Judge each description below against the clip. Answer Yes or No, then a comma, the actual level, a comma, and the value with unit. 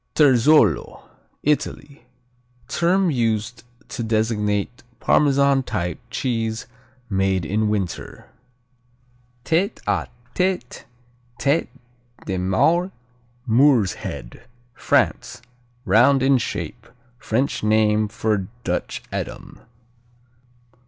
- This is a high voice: No, low, 115 Hz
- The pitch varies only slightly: No, average, 4.7 semitones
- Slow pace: Yes, slow, 85 wpm